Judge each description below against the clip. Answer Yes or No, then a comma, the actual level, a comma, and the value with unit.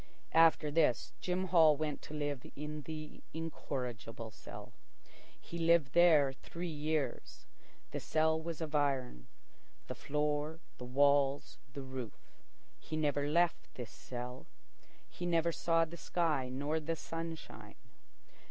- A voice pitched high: No, medium, 150 Hz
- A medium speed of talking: No, slow, 130 wpm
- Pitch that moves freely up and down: No, average, 3.0 semitones